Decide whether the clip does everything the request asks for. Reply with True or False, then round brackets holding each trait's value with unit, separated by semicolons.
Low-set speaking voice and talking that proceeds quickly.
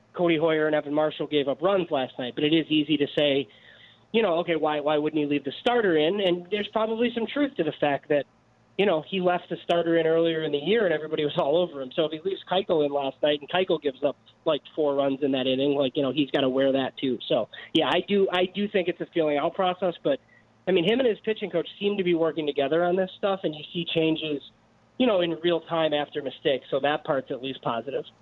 False (155 Hz; 265 wpm)